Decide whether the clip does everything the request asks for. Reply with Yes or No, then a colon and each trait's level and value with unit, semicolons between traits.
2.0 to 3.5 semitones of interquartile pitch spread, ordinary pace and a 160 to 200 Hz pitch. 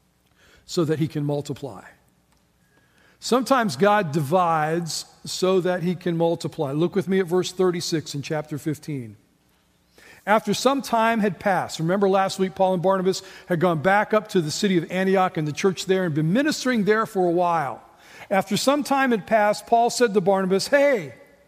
No: average, 4.5 semitones; average, 175 wpm; medium, 185 Hz